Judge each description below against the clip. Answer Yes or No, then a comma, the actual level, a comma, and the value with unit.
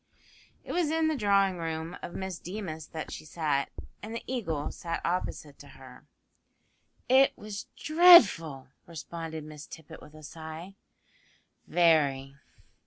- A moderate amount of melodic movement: Yes, average, 4.7 semitones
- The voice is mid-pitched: Yes, medium, 165 Hz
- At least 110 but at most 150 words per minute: Yes, average, 140 wpm